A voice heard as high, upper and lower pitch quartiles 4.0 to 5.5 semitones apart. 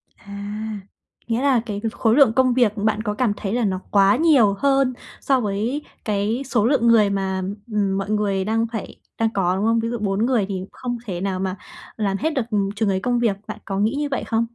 No: high, 215 Hz; average, 3.2 semitones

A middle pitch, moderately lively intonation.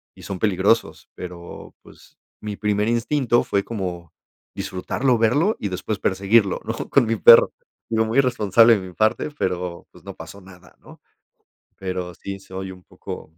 No: low, 100 Hz; average, 3.7 semitones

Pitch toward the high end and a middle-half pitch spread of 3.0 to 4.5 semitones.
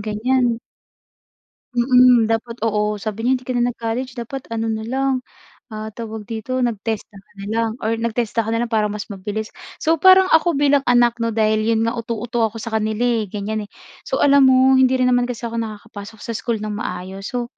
No: high, 230 Hz; narrow, 2.4 semitones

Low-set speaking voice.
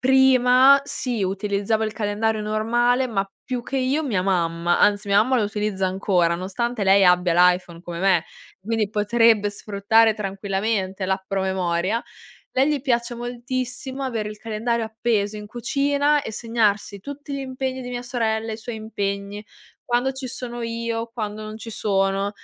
No: high, 220 Hz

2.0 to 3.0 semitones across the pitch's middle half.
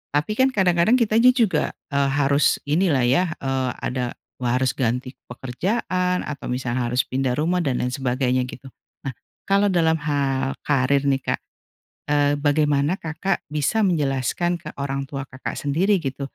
No: average, 4.8 semitones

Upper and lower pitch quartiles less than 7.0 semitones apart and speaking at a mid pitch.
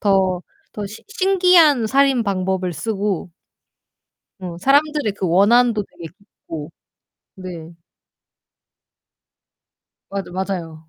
No: average, 5.2 semitones; high, 200 Hz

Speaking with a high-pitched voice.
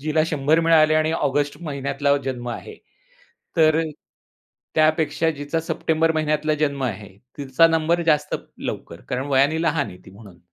No: medium, 150 Hz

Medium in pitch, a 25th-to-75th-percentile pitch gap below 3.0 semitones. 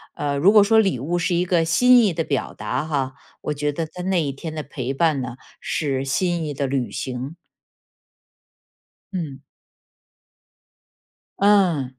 No: medium, 155 Hz; average, 4.5 semitones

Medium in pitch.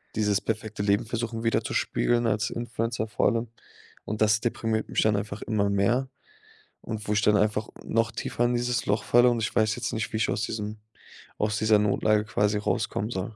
No: low, 110 Hz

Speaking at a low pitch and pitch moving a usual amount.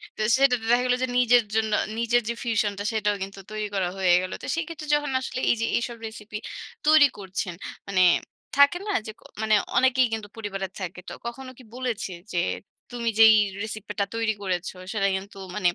No: high, 220 Hz; average, 3.7 semitones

